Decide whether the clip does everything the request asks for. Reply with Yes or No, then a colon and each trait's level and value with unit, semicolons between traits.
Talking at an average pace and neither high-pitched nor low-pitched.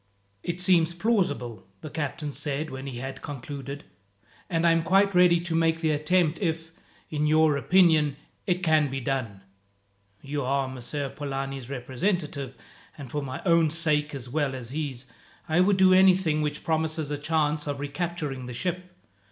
Yes: average, 165 wpm; medium, 150 Hz